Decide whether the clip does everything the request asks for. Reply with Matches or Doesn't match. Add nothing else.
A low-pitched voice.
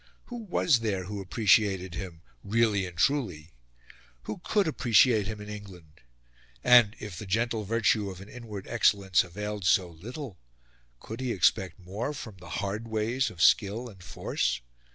Matches